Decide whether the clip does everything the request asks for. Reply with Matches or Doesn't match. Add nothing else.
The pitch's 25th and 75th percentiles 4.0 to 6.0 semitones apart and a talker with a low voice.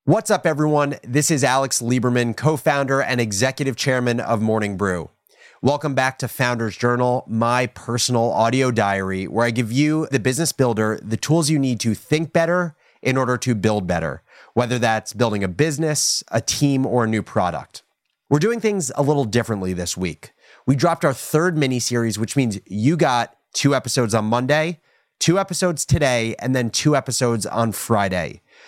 Matches